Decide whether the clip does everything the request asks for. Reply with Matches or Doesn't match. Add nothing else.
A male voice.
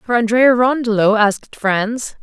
Doesn't match